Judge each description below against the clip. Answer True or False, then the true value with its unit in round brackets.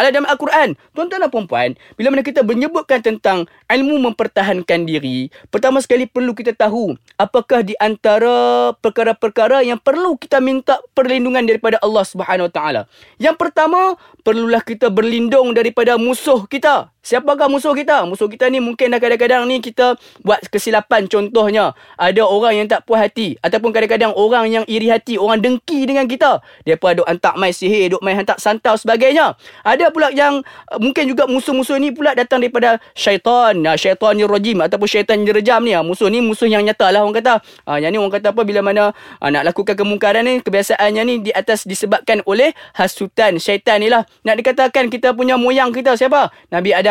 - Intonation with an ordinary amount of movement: True (3.8 semitones)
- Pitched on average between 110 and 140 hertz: False (230 Hz)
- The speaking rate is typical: False (175 wpm)